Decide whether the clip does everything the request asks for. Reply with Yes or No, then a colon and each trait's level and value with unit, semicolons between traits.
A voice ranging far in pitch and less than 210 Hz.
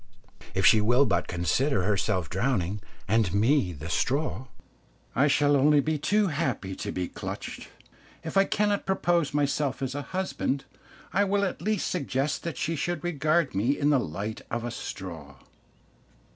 Yes: wide, 7.2 semitones; low, 135 Hz